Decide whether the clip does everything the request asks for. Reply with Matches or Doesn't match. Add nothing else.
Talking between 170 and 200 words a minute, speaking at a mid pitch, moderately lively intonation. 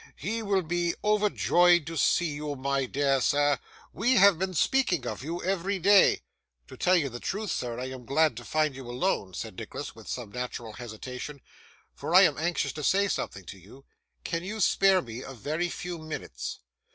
Doesn't match